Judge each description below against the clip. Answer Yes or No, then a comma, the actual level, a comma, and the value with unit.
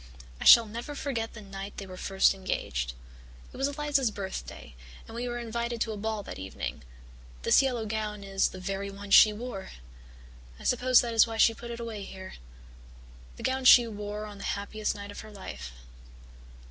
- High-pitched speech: Yes, high, 215 Hz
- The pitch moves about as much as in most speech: Yes, average, 3.1 semitones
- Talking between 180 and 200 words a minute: Yes, average, 190 wpm